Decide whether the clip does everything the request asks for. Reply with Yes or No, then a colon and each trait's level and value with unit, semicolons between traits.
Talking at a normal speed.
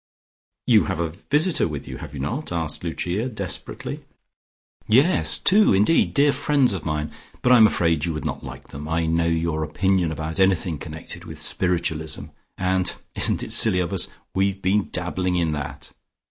Yes: average, 175 wpm